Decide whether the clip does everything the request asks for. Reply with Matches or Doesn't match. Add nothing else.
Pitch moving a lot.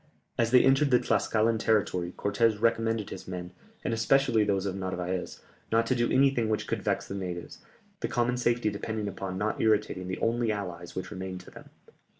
Doesn't match